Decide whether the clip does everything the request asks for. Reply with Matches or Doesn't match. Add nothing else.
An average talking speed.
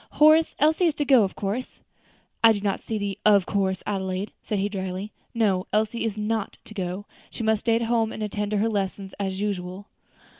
Doesn't match